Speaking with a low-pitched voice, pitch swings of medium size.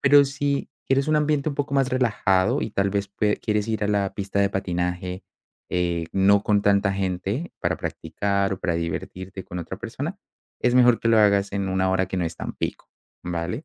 Yes: low, 100 Hz; average, 4.6 semitones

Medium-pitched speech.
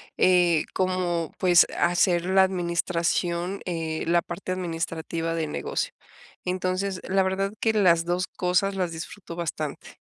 Yes: medium, 175 Hz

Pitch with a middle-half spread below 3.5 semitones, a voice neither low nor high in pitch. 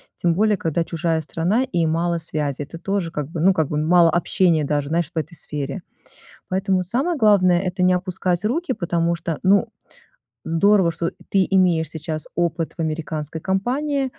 Yes: average, 2.9 semitones; medium, 170 Hz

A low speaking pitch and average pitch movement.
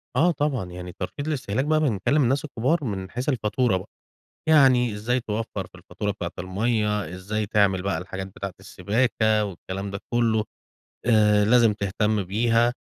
Yes: low, 110 Hz; average, 3.8 semitones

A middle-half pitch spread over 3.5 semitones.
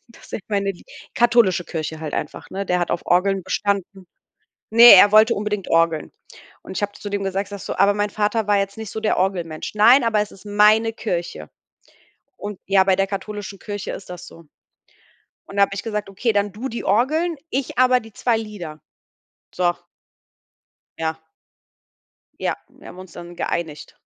No: average, 2.8 semitones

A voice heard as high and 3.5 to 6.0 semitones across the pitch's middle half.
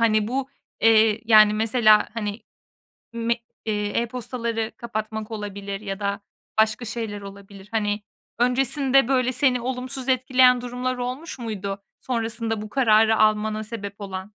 No: high, 225 Hz; average, 2.9 semitones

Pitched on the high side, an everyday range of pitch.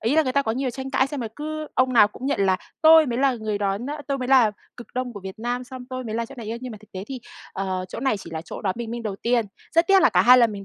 Yes: high, 240 Hz; average, 4.0 semitones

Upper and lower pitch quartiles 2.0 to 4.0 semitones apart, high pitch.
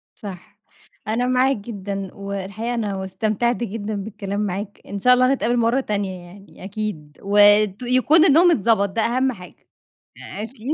Yes: average, 3.5 semitones; high, 210 Hz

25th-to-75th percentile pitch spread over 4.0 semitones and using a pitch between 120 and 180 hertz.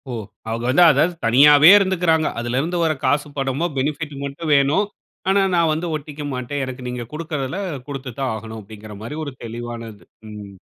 Yes: average, 4.7 semitones; medium, 140 Hz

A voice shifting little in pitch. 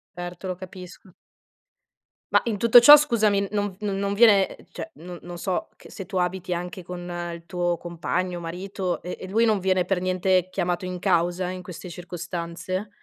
Yes: narrow, 1.9 semitones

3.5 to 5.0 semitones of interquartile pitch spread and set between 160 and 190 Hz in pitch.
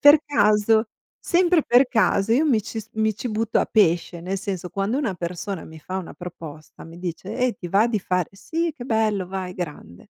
No: average, 4.5 semitones; high, 205 Hz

